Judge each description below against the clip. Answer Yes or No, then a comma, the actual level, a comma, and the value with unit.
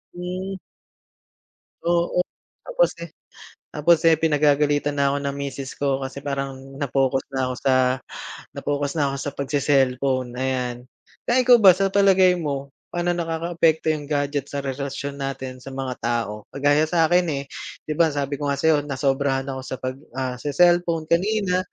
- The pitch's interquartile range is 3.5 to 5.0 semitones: Yes, average, 3.8 semitones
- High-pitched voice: No, medium, 145 Hz